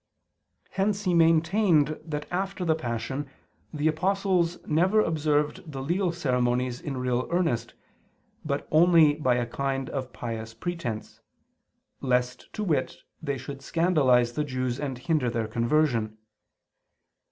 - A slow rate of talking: Yes, slow, 130 wpm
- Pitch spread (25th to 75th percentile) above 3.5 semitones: Yes, average, 5.1 semitones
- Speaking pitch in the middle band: Yes, medium, 145 Hz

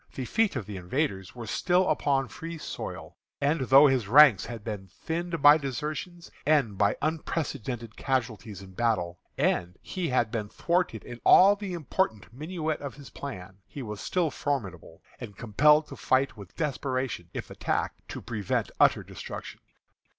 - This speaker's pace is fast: No, average, 160 wpm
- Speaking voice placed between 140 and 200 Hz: No, low, 130 Hz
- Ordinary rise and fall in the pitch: No, wide, 6.4 semitones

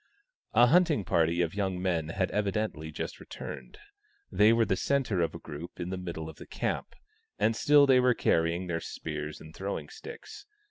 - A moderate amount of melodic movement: No, wide, 5.7 semitones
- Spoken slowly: No, average, 185 wpm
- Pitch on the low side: Yes, very low, 95 Hz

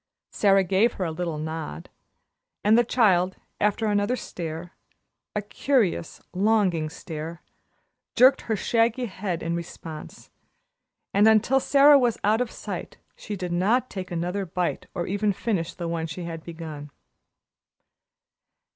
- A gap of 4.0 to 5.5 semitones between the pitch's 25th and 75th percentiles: Yes, average, 4.7 semitones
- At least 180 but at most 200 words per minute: No, average, 140 wpm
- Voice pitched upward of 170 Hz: Yes, high, 190 Hz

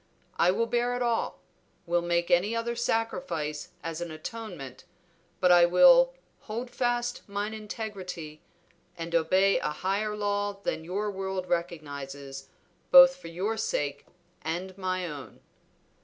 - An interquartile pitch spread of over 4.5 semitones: Yes, average, 5.2 semitones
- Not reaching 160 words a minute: Yes, slow, 135 wpm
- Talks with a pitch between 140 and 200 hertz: Yes, high, 190 Hz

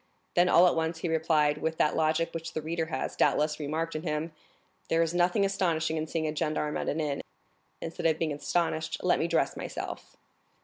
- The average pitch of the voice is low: No, medium, 160 Hz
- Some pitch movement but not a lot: No, narrow, 1.3 semitones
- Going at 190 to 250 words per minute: Yes, fast, 205 wpm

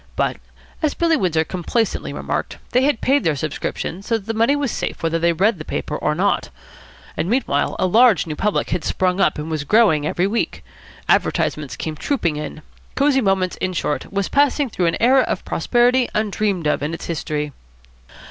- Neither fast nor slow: Yes, average, 190 wpm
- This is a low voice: No, high, 190 Hz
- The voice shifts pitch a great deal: Yes, wide, 7.0 semitones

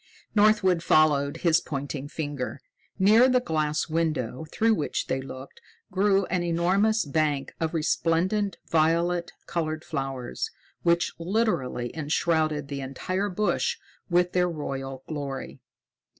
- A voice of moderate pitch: Yes, medium, 160 Hz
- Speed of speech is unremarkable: No, slow, 120 wpm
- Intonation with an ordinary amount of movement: Yes, average, 4.4 semitones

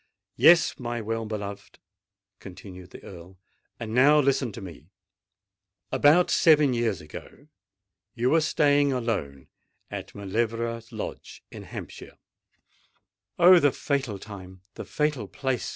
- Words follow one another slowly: Yes, slow, 120 wpm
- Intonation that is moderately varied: No, wide, 6.3 semitones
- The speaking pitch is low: Yes, low, 115 Hz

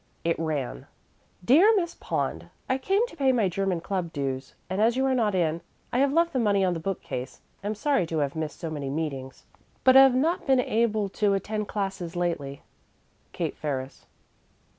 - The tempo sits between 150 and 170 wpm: No, average, 185 wpm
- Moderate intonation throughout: No, wide, 8.3 semitones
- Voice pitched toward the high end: Yes, high, 195 Hz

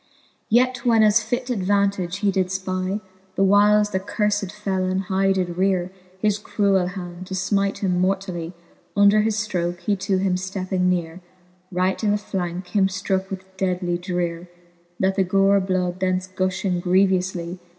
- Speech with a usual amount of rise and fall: No, narrow, 1.7 semitones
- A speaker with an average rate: Yes, average, 160 wpm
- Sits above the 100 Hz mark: Yes, high, 190 Hz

